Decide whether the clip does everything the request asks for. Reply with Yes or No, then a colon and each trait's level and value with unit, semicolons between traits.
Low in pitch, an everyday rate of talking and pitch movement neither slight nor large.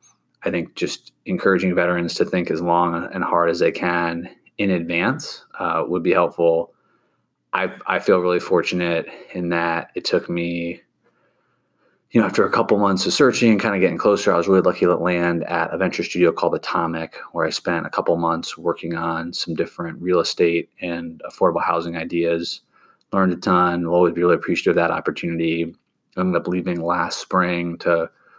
No: very low, 85 Hz; average, 190 wpm; narrow, 1.0 semitones